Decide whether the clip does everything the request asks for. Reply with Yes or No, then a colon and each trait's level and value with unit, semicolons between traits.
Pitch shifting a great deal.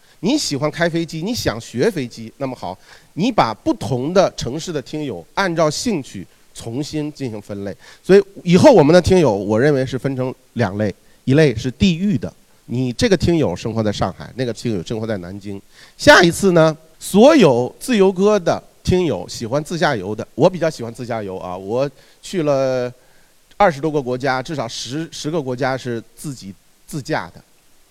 Yes: wide, 6.3 semitones